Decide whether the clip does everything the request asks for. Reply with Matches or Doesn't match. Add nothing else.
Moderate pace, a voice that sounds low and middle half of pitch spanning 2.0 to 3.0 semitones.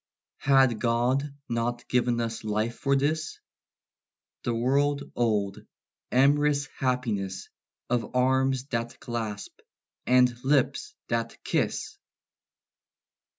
Doesn't match